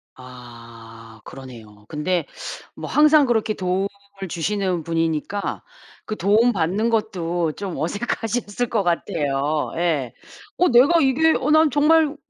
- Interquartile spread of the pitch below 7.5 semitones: No, wide, 8.0 semitones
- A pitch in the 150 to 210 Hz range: Yes, medium, 185 Hz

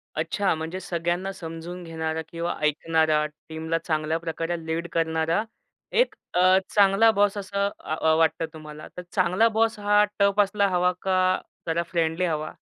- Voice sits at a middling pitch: Yes, medium, 170 Hz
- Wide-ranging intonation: No, average, 3.2 semitones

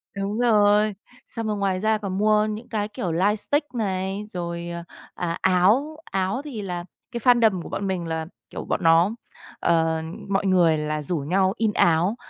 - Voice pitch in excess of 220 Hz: No, high, 195 Hz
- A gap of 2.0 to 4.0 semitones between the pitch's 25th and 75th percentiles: Yes, average, 3.7 semitones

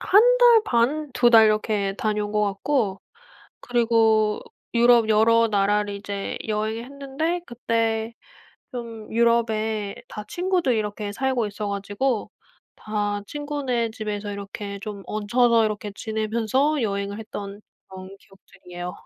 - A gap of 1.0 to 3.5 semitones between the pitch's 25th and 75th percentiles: Yes, average, 2.7 semitones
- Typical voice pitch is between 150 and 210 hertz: No, high, 220 Hz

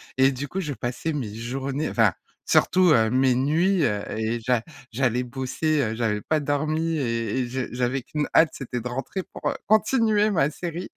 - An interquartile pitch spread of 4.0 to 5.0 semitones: Yes, average, 4.5 semitones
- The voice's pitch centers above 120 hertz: Yes, low, 135 Hz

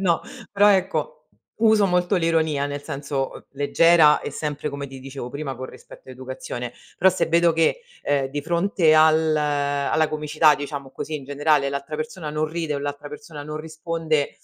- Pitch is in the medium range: Yes, medium, 150 Hz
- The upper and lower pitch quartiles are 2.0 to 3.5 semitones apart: Yes, narrow, 2.6 semitones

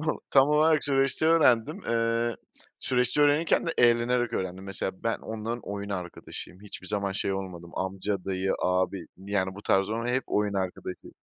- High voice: No, low, 105 Hz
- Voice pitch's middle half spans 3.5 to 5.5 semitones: Yes, average, 4.6 semitones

